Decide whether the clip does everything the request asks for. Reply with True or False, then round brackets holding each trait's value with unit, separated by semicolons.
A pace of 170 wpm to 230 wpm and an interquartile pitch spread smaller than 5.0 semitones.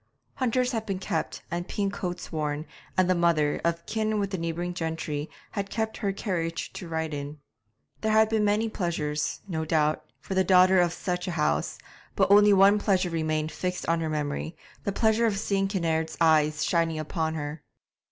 True (185 wpm; 4.0 semitones)